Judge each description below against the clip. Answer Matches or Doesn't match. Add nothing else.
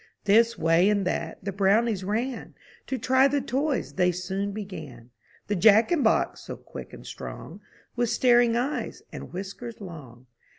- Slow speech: Doesn't match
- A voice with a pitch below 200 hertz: Doesn't match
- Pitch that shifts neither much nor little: Matches